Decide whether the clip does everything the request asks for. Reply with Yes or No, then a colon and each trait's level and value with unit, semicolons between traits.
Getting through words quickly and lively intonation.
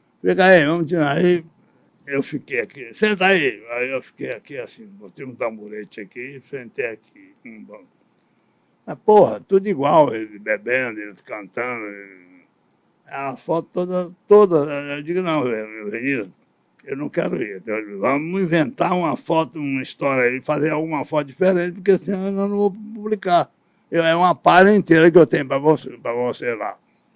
No: average, 165 wpm; wide, 6.4 semitones